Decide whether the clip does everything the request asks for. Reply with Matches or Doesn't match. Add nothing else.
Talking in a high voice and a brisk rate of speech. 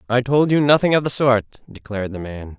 Doesn't match